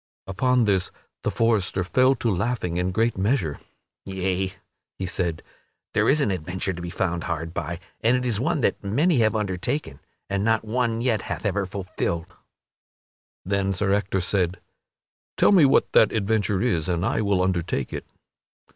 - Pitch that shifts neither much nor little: Yes, average, 3.9 semitones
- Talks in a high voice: No, low, 100 Hz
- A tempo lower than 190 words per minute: Yes, average, 165 wpm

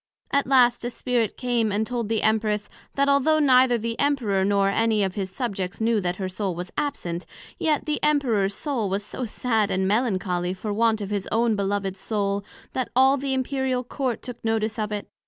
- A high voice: Yes, high, 220 Hz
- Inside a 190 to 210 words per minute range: Yes, average, 195 wpm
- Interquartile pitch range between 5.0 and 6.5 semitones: No, average, 4.1 semitones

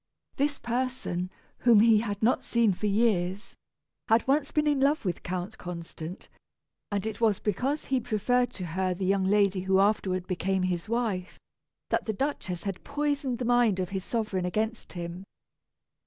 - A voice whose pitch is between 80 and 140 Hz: No, high, 210 Hz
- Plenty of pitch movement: No, average, 4.6 semitones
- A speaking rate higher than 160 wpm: Yes, average, 170 wpm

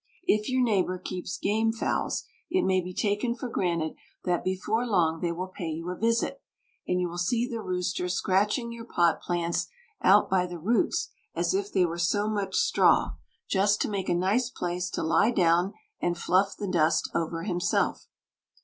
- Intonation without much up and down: No, average, 3.7 semitones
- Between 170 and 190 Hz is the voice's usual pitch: Yes, medium, 185 Hz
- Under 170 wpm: No, average, 185 wpm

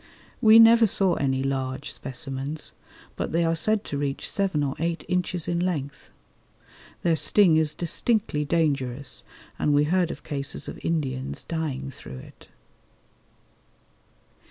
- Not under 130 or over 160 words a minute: Yes, slow, 135 wpm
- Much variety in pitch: No, average, 4.2 semitones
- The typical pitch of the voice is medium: Yes, medium, 150 Hz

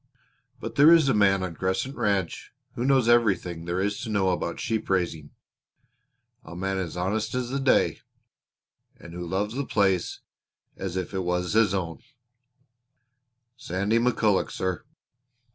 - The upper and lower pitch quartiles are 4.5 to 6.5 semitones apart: No, average, 4.0 semitones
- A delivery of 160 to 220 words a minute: No, average, 145 wpm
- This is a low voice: Yes, very low, 95 Hz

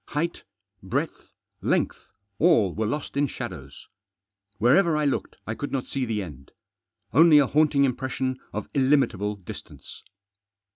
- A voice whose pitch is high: No, low, 135 Hz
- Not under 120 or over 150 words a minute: Yes, slow, 135 wpm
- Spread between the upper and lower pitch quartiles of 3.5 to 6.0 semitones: Yes, average, 5.2 semitones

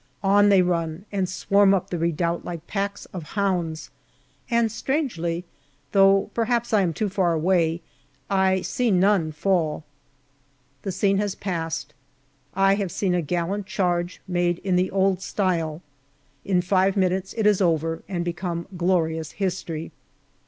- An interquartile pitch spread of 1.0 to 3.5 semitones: Yes, narrow, 2.6 semitones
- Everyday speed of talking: Yes, average, 145 wpm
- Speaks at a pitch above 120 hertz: Yes, medium, 185 Hz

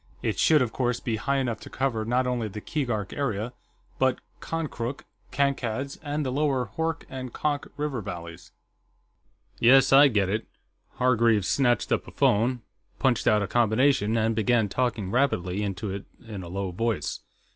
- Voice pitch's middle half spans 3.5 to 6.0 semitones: Yes, average, 4.1 semitones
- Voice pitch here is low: Yes, low, 120 Hz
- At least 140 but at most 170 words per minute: Yes, average, 165 wpm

